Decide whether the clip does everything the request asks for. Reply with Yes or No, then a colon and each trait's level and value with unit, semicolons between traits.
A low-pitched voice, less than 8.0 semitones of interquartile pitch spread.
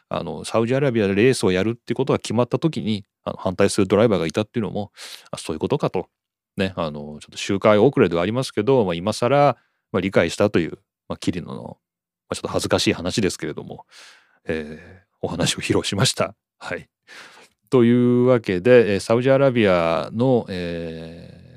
Yes: low, 110 Hz; average, 5.2 semitones